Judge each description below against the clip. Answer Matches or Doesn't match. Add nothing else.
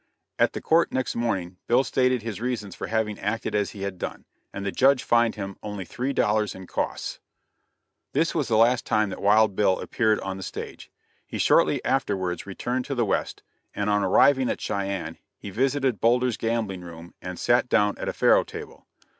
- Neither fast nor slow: Matches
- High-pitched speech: Doesn't match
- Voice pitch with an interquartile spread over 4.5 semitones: Doesn't match